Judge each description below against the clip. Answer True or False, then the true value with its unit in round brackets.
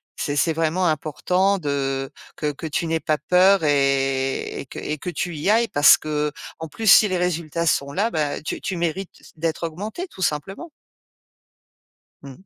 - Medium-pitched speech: True (160 Hz)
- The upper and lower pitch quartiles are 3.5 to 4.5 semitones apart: True (3.9 semitones)